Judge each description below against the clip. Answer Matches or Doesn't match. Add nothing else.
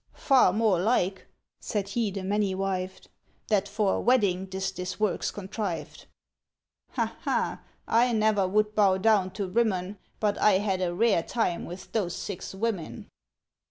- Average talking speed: Matches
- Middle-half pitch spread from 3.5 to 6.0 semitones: Doesn't match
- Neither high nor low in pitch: Doesn't match